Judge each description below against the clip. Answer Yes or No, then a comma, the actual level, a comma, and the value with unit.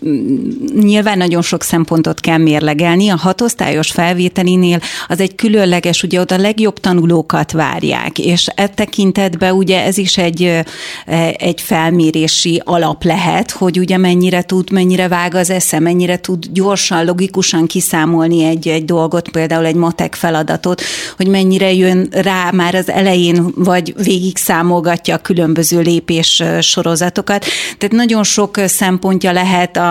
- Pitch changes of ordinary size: No, narrow, 2.1 semitones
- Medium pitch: Yes, medium, 180 Hz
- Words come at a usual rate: Yes, average, 140 wpm